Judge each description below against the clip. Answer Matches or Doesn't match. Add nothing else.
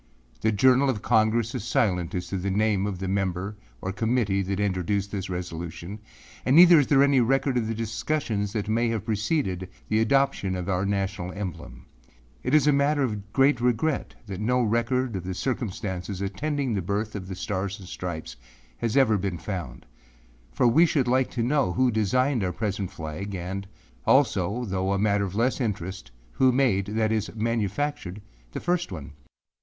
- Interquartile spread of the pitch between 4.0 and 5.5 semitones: Matches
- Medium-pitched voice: Doesn't match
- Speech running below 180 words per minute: Doesn't match